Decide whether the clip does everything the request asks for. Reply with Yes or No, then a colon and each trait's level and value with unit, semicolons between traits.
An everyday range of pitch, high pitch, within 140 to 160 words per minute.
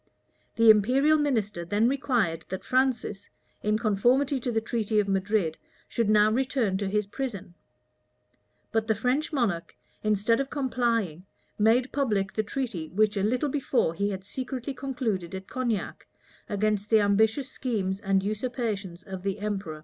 Yes: average, 4.2 semitones; high, 215 Hz; average, 150 wpm